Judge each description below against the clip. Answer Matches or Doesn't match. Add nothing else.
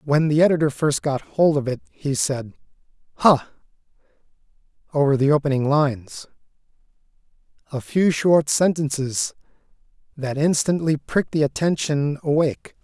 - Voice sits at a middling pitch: Matches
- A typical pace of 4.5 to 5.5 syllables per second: Matches